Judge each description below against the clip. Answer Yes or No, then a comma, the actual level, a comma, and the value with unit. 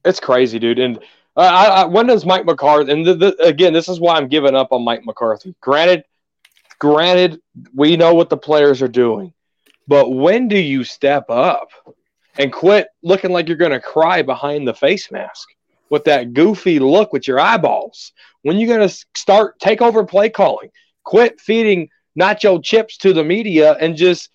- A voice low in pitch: No, medium, 170 Hz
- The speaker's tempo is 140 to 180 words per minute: No, average, 190 wpm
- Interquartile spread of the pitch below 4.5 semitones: No, average, 5.0 semitones